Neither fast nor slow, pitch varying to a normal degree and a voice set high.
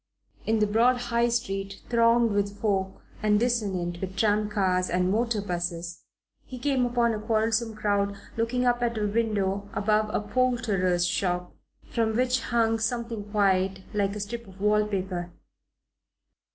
Yes: average, 150 wpm; average, 3.1 semitones; high, 210 Hz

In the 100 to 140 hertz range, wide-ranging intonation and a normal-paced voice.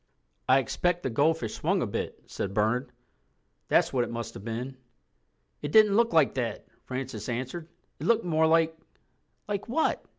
Yes: low, 135 Hz; wide, 5.9 semitones; average, 165 wpm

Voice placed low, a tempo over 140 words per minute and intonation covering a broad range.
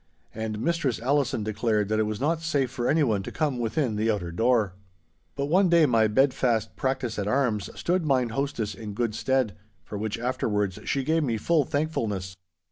No: low, 120 Hz; average, 190 wpm; average, 4.8 semitones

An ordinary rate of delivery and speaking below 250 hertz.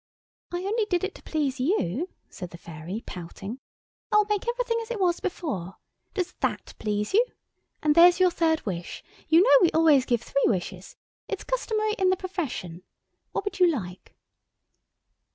No: average, 170 wpm; very high, 330 Hz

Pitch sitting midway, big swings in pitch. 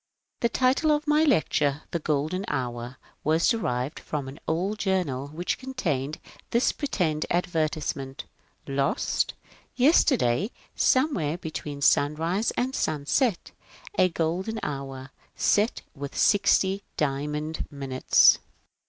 Yes: medium, 160 Hz; wide, 6.8 semitones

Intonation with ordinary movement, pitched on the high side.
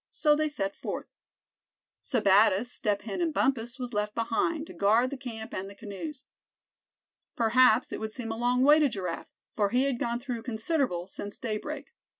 Yes: average, 3.9 semitones; high, 235 Hz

